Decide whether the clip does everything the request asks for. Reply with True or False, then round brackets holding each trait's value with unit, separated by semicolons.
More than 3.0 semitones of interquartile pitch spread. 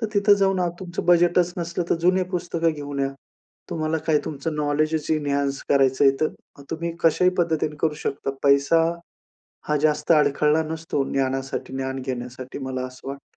True (3.4 semitones)